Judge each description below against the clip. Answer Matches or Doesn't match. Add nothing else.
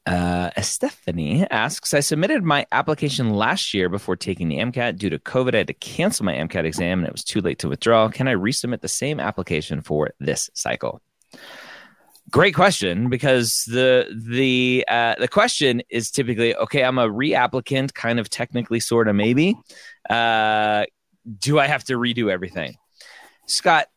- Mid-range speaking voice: Doesn't match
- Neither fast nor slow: Matches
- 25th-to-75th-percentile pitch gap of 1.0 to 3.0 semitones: Doesn't match